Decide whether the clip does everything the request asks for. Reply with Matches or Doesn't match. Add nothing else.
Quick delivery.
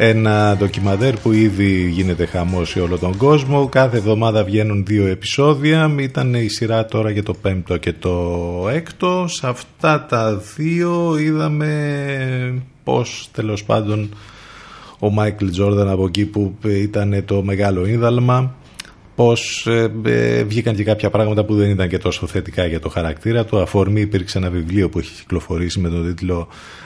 Doesn't match